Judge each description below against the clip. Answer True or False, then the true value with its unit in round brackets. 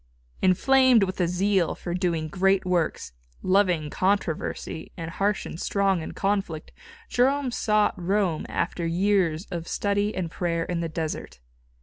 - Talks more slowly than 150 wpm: True (140 wpm)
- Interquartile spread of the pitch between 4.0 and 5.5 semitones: False (3.3 semitones)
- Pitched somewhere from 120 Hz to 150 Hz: False (185 Hz)